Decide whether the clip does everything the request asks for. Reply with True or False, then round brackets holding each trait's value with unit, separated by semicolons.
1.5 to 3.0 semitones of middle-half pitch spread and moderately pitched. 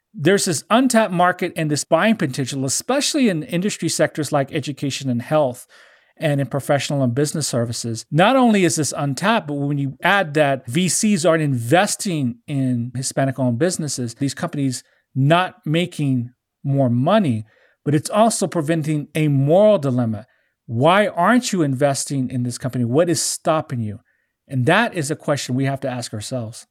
False (4.6 semitones; 145 Hz)